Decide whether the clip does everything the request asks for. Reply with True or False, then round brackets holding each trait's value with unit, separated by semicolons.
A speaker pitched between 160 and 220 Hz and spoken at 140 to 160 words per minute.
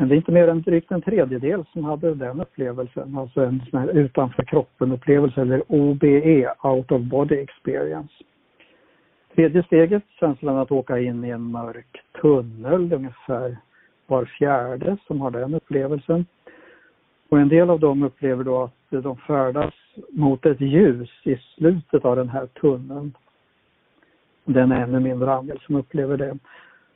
False (140 Hz; 155 wpm)